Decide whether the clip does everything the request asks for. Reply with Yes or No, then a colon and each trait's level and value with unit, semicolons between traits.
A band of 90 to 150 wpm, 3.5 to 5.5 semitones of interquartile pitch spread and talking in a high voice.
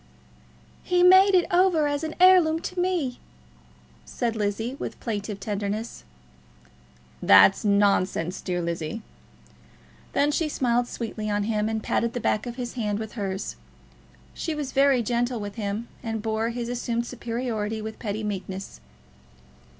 Yes: average, 140 wpm; average, 4.0 semitones; high, 230 Hz